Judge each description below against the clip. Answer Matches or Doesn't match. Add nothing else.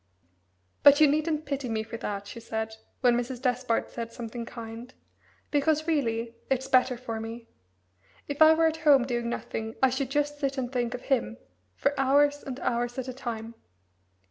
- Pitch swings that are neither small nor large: Matches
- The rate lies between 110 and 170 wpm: Doesn't match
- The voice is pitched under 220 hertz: Doesn't match